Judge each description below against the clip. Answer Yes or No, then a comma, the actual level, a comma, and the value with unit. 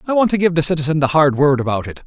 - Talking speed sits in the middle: No, fast, 320 wpm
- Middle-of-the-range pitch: Yes, medium, 155 Hz